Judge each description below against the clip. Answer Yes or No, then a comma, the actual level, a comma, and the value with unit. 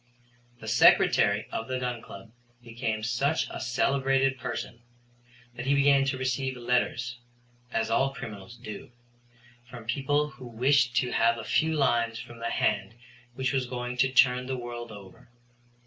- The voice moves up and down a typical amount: No, narrow, 2.3 semitones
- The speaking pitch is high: No, low, 125 Hz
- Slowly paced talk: No, average, 155 wpm